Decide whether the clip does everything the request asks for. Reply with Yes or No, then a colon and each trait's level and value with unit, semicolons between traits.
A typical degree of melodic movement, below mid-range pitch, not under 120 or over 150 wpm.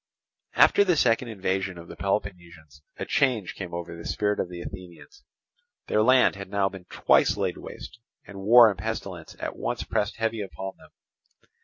No: average, 4.0 semitones; low, 100 Hz; average, 175 wpm